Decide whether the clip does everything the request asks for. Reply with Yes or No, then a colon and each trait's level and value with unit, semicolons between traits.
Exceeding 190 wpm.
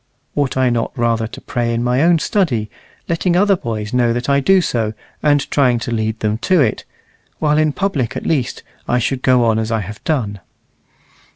Yes: average, 200 wpm